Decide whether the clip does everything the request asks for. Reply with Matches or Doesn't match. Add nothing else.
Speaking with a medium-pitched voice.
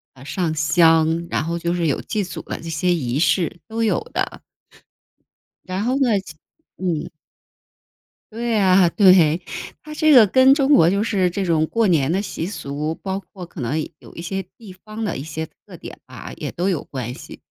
Matches